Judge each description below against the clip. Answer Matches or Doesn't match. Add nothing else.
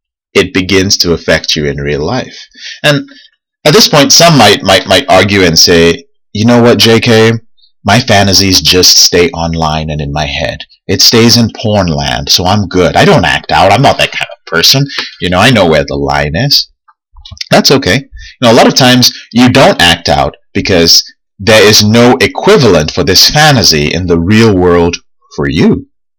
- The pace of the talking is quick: Doesn't match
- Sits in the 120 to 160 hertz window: Doesn't match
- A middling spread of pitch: Doesn't match